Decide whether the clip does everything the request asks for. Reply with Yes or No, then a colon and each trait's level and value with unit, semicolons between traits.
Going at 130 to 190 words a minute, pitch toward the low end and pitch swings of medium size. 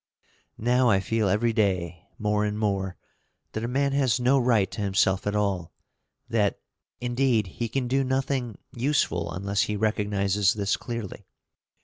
Yes: average, 150 wpm; low, 105 Hz; average, 3.7 semitones